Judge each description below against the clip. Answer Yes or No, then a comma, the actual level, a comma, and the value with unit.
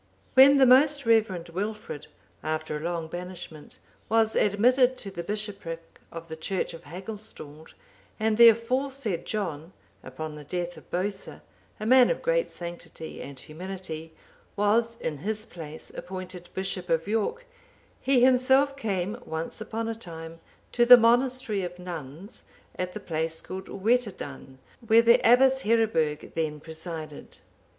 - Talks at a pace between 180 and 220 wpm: No, average, 145 wpm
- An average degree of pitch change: No, wide, 5.9 semitones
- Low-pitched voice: No, high, 190 Hz